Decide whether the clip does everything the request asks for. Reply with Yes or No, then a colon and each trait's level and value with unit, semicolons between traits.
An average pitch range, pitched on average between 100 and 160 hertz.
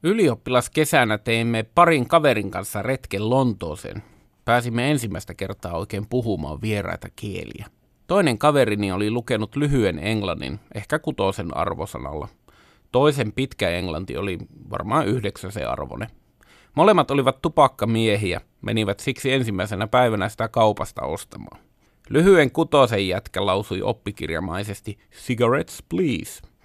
Yes: average, 4.9 semitones; low, 110 Hz